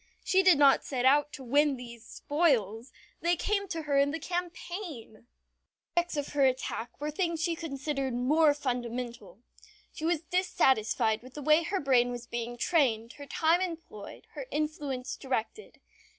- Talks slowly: No, average, 165 wpm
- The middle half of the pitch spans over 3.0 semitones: Yes, average, 4.9 semitones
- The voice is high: Yes, very high, 285 Hz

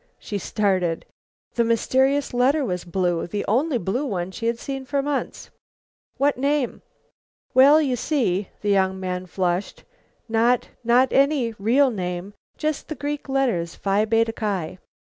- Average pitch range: No, wide, 6.2 semitones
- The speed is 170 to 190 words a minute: No, average, 145 wpm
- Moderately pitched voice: No, high, 230 Hz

